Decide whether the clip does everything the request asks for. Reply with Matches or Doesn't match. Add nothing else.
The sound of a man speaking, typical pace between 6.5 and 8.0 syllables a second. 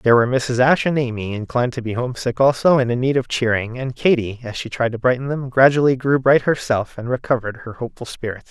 Matches